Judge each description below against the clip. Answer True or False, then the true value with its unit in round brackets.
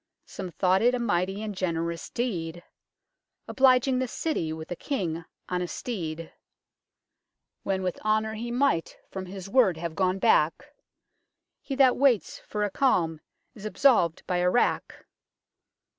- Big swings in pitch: True (5.8 semitones)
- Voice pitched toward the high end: True (195 Hz)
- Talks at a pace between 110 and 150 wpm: True (145 wpm)